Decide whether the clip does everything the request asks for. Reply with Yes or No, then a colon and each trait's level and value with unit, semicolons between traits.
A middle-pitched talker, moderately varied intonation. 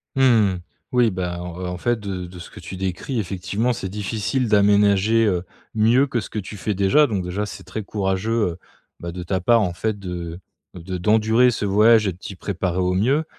No: low, 100 Hz; average, 3.4 semitones